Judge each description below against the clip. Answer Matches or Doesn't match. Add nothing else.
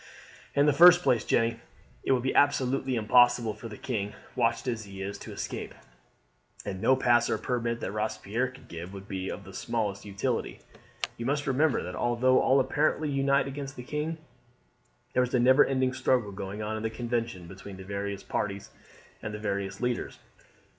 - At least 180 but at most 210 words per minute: Matches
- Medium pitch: Doesn't match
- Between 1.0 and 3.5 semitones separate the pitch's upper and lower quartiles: Doesn't match